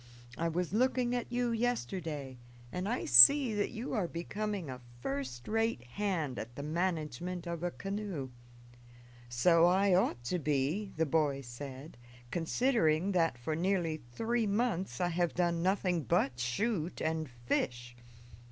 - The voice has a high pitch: No, medium, 170 Hz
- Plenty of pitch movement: Yes, wide, 6.2 semitones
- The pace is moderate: Yes, average, 145 wpm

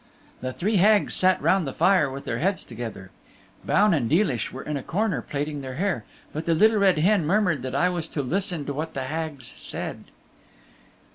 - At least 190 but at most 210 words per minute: Yes, average, 200 wpm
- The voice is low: No, medium, 160 Hz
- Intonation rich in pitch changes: Yes, wide, 5.9 semitones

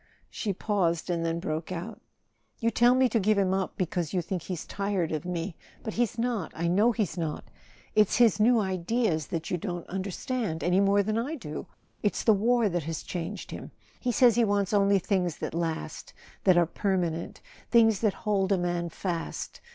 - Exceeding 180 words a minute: Yes, average, 190 wpm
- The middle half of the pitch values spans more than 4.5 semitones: No, average, 3.9 semitones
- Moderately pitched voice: No, high, 195 Hz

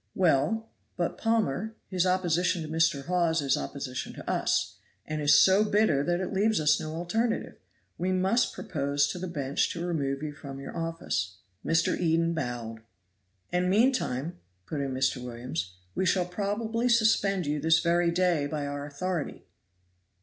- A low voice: No, medium, 165 Hz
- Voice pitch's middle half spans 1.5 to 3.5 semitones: No, average, 4.7 semitones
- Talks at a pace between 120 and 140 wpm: No, average, 160 wpm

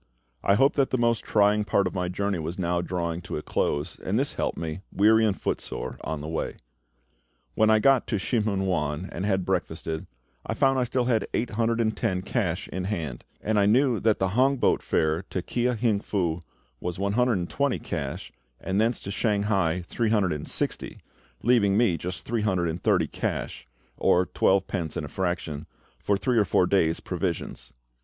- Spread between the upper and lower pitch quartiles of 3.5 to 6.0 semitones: Yes, average, 4.3 semitones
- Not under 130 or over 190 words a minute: No, average, 200 wpm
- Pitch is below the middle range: Yes, low, 100 Hz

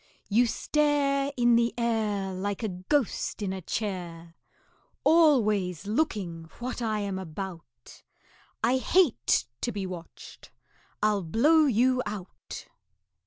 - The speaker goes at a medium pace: No, slow, 120 wpm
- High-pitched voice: Yes, high, 210 Hz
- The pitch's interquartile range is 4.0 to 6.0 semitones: Yes, average, 5.2 semitones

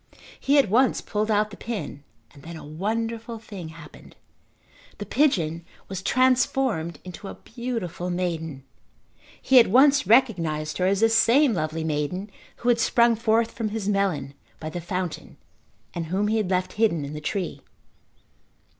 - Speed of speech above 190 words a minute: No, average, 160 wpm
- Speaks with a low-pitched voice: No, high, 200 Hz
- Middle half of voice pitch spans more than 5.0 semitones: Yes, wide, 5.6 semitones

